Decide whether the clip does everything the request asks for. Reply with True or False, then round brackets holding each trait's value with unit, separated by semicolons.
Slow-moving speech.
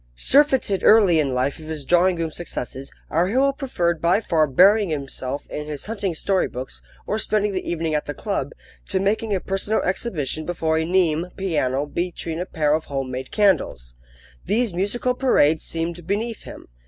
False (180 wpm)